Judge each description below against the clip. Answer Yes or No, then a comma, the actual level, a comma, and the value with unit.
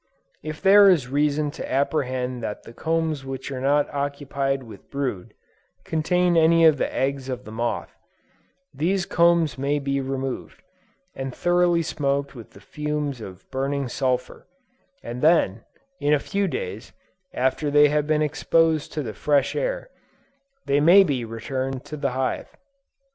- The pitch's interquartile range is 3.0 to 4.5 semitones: Yes, average, 3.3 semitones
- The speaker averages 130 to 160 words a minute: Yes, average, 155 wpm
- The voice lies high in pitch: No, medium, 140 Hz